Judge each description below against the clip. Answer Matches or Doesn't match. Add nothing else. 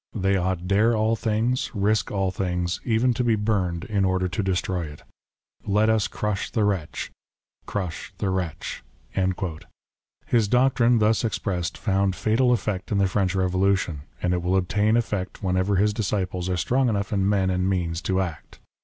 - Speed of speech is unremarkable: Matches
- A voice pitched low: Matches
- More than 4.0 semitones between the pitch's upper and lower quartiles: Doesn't match